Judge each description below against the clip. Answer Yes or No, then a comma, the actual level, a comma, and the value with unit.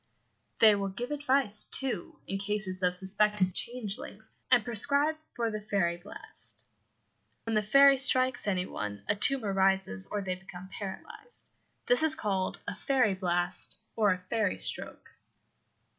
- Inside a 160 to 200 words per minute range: No, average, 145 wpm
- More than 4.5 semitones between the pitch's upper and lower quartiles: Yes, average, 4.9 semitones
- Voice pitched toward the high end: Yes, high, 210 Hz